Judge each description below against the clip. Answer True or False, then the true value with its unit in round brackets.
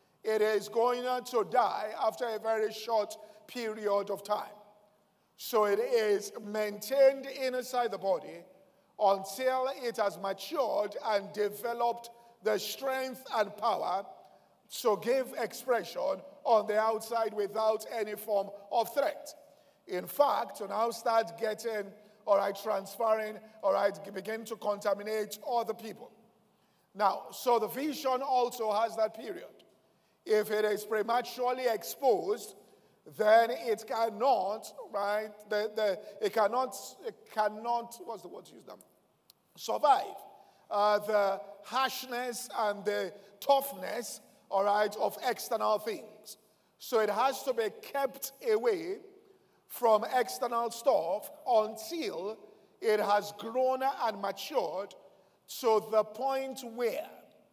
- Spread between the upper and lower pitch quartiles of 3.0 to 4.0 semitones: True (3.5 semitones)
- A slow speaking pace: True (125 wpm)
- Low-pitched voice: False (220 Hz)